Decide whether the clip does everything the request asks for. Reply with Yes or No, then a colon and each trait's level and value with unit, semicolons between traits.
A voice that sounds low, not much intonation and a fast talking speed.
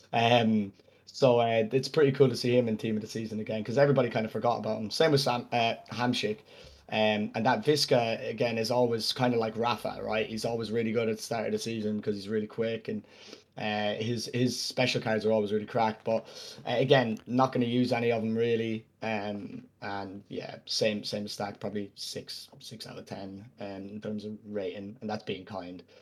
Yes: low, 110 Hz; narrow, 2.0 semitones; fast, 215 wpm